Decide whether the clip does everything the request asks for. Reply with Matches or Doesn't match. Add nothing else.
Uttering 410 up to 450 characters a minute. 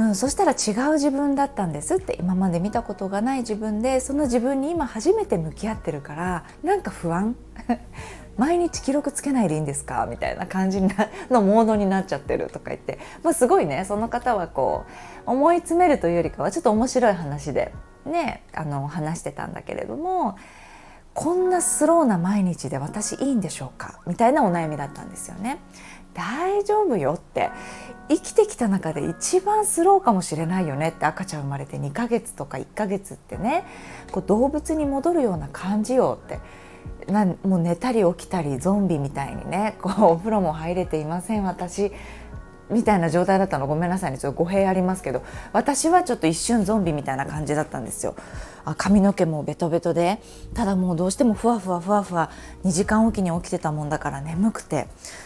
Doesn't match